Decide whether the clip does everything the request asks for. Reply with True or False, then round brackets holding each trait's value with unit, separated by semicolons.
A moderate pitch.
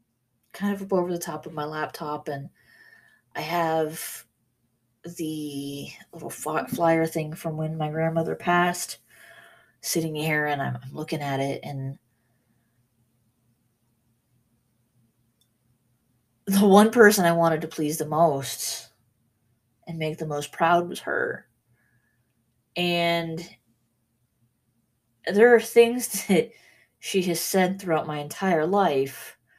True (145 Hz)